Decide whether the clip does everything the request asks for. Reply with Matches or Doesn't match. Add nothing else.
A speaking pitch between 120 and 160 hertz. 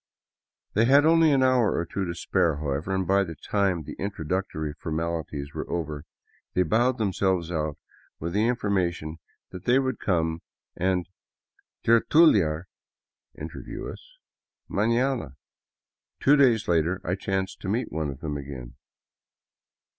Doesn't match